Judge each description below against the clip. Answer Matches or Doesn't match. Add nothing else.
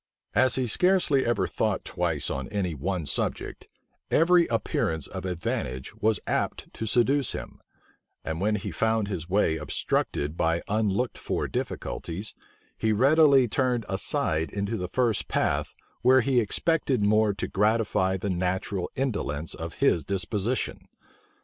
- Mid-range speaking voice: Doesn't match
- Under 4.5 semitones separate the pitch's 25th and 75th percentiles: Doesn't match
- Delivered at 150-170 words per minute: Doesn't match